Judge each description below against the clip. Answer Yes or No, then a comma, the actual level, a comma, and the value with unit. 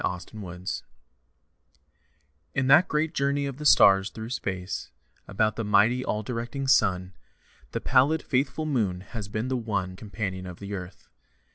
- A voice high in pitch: No, low, 110 Hz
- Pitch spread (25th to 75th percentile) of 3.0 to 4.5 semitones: No, wide, 5.5 semitones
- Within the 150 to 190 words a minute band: Yes, average, 155 wpm